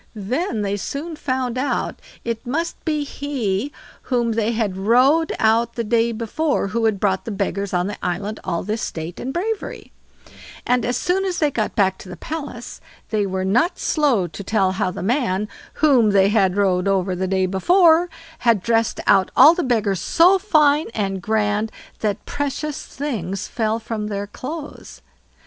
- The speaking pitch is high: Yes, high, 225 Hz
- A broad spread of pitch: Yes, wide, 6.3 semitones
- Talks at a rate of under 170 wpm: No, average, 175 wpm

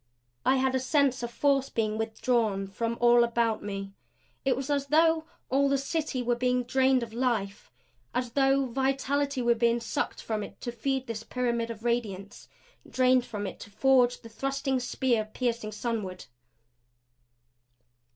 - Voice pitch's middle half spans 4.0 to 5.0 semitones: No, average, 2.9 semitones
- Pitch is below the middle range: No, high, 245 Hz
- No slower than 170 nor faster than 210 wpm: No, average, 160 wpm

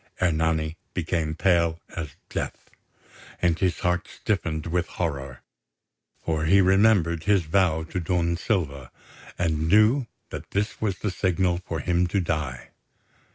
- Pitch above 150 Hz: No, very low, 85 Hz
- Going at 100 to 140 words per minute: Yes, slow, 135 wpm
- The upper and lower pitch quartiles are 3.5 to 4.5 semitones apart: No, average, 2.8 semitones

